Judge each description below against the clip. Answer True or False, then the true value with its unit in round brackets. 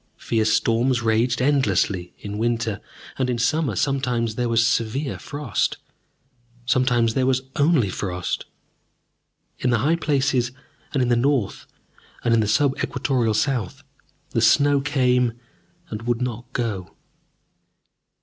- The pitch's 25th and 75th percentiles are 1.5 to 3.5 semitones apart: True (3.0 semitones)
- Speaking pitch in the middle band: False (120 Hz)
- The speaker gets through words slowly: True (130 wpm)